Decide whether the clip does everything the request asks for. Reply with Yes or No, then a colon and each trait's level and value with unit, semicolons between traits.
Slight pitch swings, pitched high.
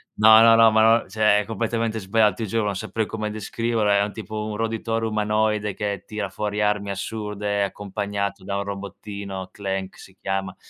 No: narrow, 1.6 semitones; low, 105 Hz